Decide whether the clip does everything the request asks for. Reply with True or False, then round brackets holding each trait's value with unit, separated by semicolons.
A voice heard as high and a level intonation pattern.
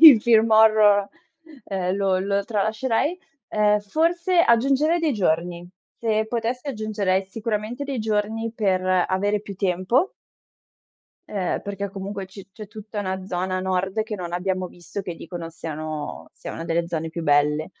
False (200 Hz; 3.2 semitones)